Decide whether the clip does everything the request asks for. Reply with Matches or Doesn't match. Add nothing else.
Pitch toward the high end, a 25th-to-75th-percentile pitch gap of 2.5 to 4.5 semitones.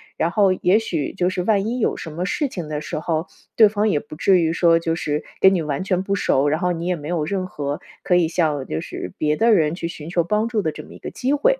Doesn't match